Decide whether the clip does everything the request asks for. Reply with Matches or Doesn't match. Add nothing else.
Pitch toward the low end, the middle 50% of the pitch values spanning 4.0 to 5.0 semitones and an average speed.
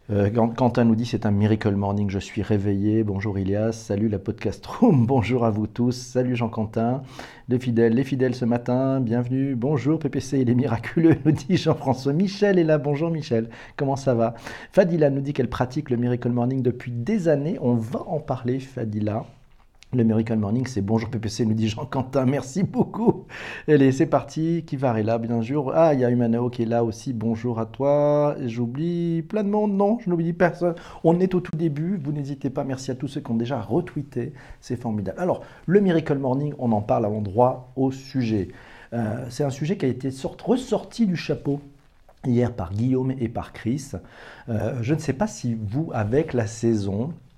Matches